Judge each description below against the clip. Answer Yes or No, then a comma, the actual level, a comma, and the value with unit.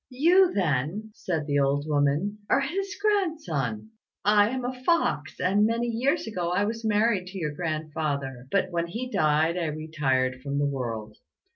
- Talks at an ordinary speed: Yes, average, 165 wpm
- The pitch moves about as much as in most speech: No, wide, 8.1 semitones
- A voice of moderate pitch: Yes, medium, 175 Hz